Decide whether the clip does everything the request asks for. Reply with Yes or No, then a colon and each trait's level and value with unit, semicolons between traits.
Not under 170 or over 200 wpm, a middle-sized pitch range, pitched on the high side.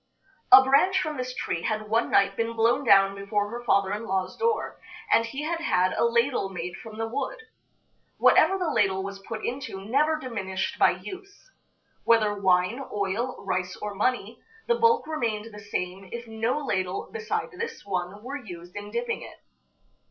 No: average, 175 wpm; wide, 5.7 semitones; high, 225 Hz